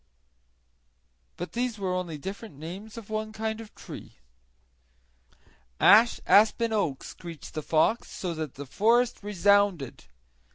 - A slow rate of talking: Yes, slow, 130 wpm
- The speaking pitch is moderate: No, high, 200 Hz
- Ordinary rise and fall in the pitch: Yes, average, 4.6 semitones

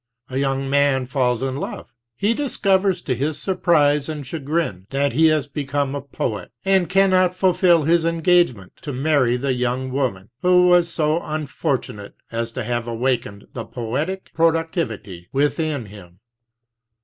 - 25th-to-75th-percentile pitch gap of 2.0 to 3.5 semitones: No, average, 5.0 semitones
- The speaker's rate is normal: Yes, average, 160 wpm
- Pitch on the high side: No, medium, 140 Hz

